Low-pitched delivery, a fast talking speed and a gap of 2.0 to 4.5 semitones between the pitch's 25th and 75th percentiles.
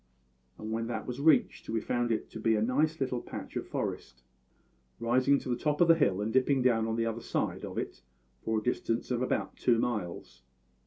Yes: low, 120 Hz; fast, 215 wpm; average, 2.7 semitones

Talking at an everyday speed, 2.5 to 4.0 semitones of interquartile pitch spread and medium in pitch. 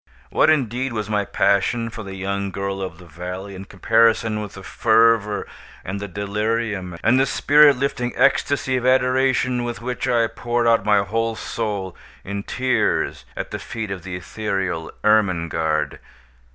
No: average, 160 wpm; average, 3.5 semitones; low, 105 Hz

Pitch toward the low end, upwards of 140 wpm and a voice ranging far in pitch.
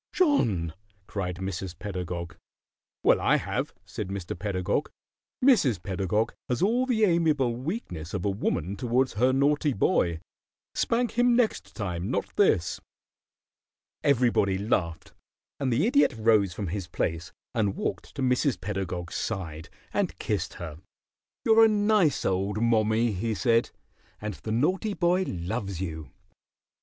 No: low, 105 Hz; slow, 135 wpm; wide, 7.6 semitones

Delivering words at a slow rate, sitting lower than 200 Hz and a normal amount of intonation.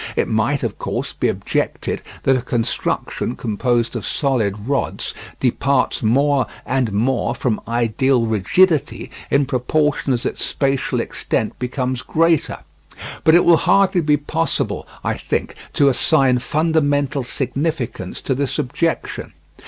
Yes: slow, 130 wpm; low, 135 Hz; average, 3.5 semitones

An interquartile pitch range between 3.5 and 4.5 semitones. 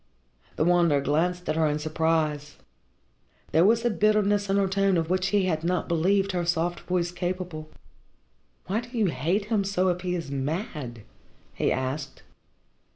Yes: average, 3.8 semitones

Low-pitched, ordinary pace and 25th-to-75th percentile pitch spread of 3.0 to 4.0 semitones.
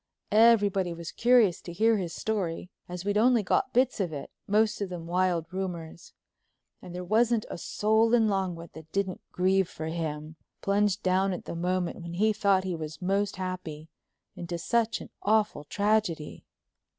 No: medium, 185 Hz; average, 170 wpm; average, 3.7 semitones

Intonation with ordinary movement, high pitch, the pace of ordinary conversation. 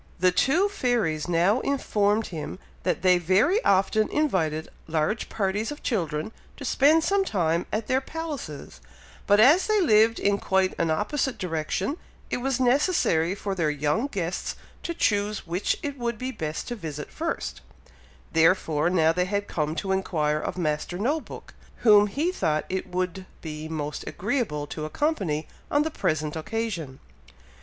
No: wide, 7.4 semitones; high, 195 Hz; average, 160 wpm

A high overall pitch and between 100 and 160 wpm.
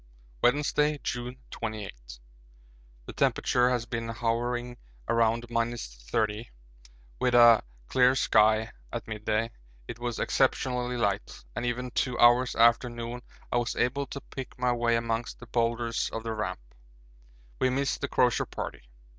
No: low, 120 Hz; average, 140 wpm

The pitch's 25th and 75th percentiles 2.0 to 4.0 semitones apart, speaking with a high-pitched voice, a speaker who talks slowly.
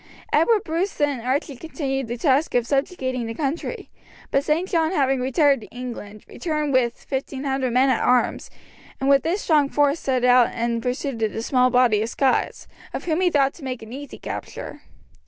No: average, 3.0 semitones; very high, 270 Hz; average, 190 wpm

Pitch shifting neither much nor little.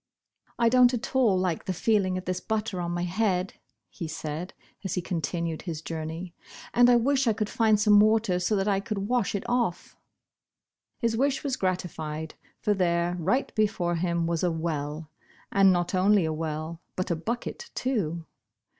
Yes: average, 4.5 semitones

